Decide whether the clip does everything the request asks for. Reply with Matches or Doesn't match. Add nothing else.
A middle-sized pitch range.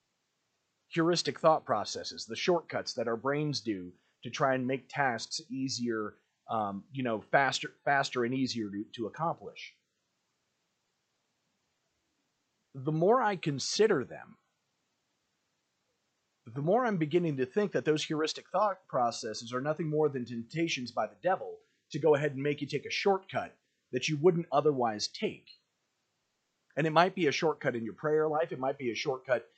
Matches